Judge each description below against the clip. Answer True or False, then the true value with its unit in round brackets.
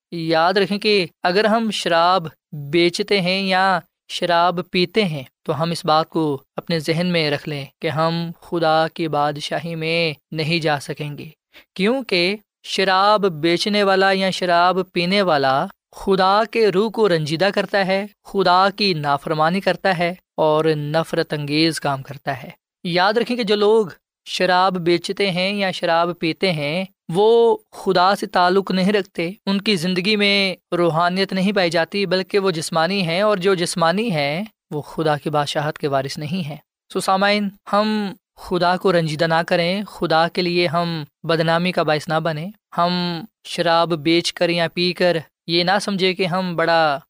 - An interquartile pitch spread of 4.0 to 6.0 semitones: False (3.1 semitones)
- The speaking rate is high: False (165 wpm)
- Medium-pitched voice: True (175 Hz)